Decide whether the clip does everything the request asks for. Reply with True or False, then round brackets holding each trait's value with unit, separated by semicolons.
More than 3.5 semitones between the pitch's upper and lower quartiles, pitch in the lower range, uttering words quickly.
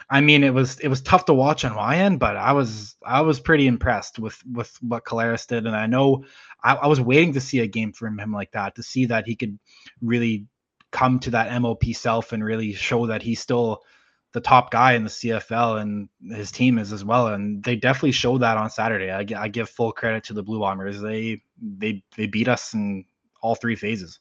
False (3.1 semitones; 115 Hz; 230 wpm)